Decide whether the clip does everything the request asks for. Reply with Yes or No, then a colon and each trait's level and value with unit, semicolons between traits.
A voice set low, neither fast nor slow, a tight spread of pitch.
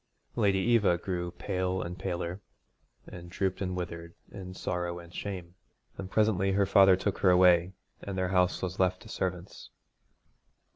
Yes: very low, 90 Hz; average, 155 wpm; narrow, 1.7 semitones